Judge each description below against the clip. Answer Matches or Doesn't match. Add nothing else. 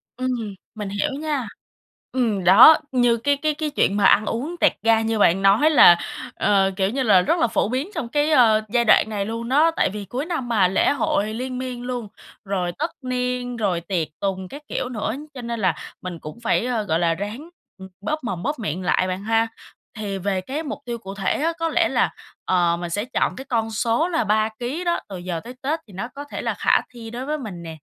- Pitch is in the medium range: Doesn't match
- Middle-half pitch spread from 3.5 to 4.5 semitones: Doesn't match